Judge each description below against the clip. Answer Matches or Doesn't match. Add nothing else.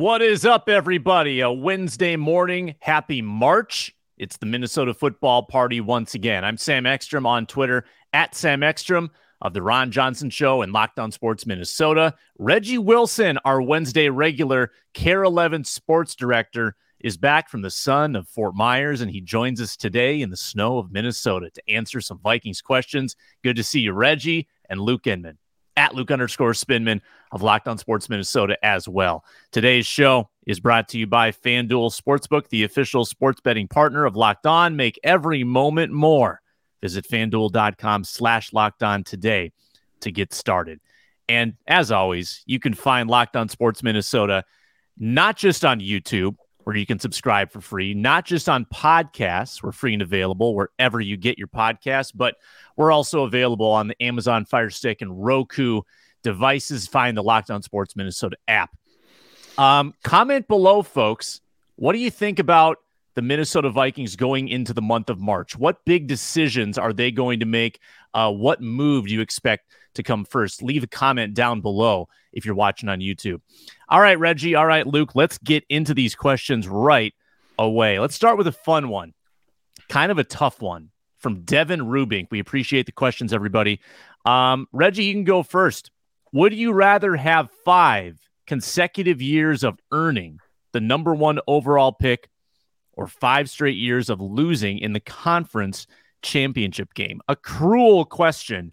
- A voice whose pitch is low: Matches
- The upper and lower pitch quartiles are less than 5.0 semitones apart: Doesn't match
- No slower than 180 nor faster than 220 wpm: Doesn't match